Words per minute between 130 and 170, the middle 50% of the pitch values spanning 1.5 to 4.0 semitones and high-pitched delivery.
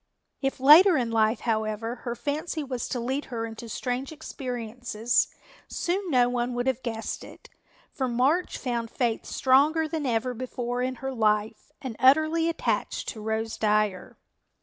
Yes: average, 155 wpm; average, 3.3 semitones; high, 245 Hz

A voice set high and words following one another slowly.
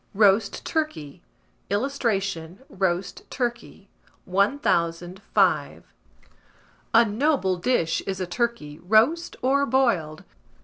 Yes: high, 200 Hz; slow, 85 wpm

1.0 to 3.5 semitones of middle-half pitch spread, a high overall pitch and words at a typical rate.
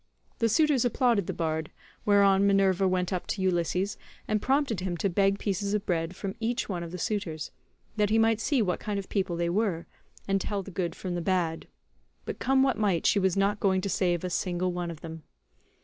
No: average, 3.0 semitones; high, 195 Hz; fast, 215 wpm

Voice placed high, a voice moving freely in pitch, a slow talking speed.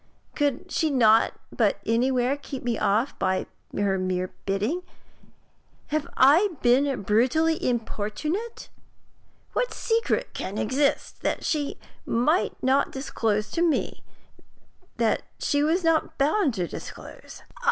Yes: very high, 265 Hz; wide, 6.1 semitones; slow, 115 wpm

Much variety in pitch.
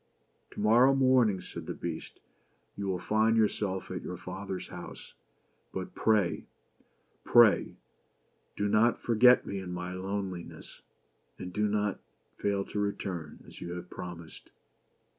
No: average, 3.1 semitones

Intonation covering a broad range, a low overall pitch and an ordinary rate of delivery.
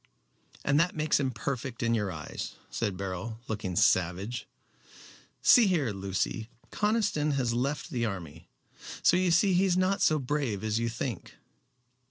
Yes: wide, 7.1 semitones; low, 120 Hz; average, 155 wpm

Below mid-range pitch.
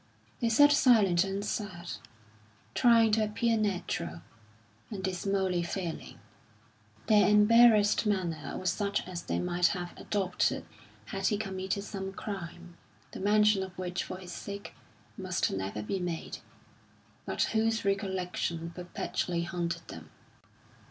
No: high, 190 Hz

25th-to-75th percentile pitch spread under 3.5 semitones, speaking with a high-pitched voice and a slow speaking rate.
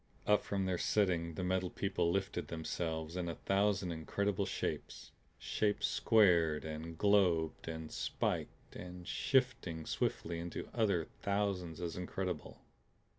No: average, 3.1 semitones; very low, 90 Hz; slow, 125 wpm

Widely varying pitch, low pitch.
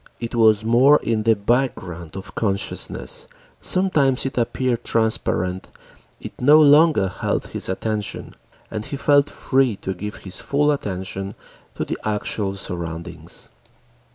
Yes: wide, 5.7 semitones; low, 110 Hz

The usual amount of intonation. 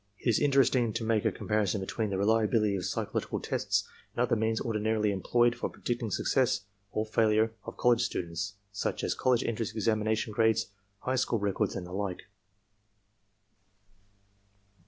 No: narrow, 2.3 semitones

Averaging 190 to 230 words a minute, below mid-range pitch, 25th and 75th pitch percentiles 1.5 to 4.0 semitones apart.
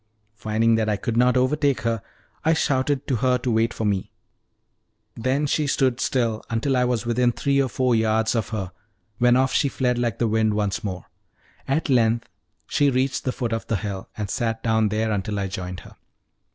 Yes: average, 200 wpm; low, 115 Hz; average, 2.9 semitones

